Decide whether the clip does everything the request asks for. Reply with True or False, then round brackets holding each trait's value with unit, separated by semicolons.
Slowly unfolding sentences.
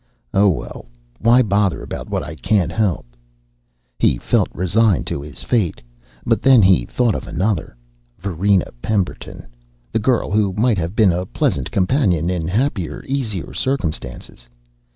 False (145 wpm)